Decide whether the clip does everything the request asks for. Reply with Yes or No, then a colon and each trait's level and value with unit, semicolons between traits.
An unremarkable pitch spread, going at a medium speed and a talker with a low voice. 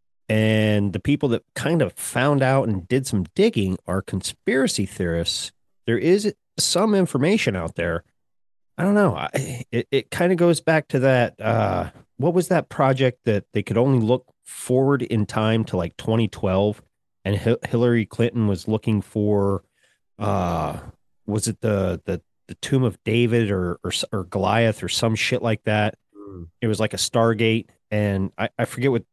Yes: average, 4.0 semitones; average, 175 wpm; low, 110 Hz